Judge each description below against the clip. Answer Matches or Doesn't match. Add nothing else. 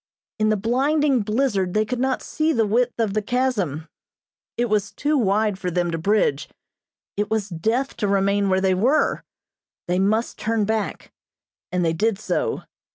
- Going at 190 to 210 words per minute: Doesn't match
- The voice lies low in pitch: Doesn't match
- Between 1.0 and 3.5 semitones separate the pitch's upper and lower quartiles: Doesn't match